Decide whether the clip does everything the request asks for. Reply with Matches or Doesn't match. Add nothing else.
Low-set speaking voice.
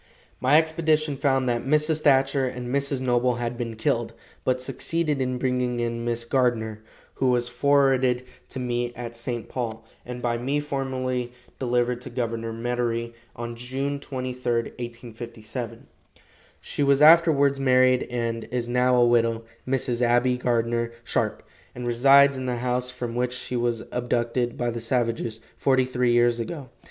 Matches